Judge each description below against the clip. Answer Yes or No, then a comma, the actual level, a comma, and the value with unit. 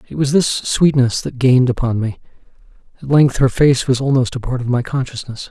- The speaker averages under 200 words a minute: No, fast, 205 wpm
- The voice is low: Yes, low, 130 Hz